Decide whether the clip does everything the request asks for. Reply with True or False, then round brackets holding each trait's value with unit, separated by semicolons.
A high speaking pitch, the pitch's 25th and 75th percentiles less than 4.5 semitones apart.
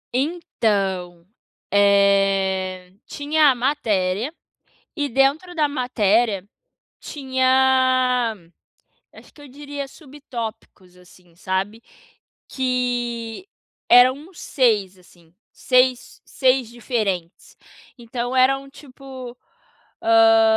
False (245 Hz; 5.0 semitones)